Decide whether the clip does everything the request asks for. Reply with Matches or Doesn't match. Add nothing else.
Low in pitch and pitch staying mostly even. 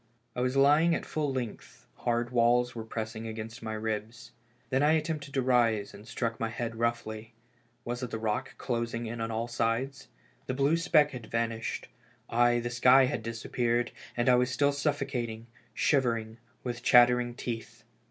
Matches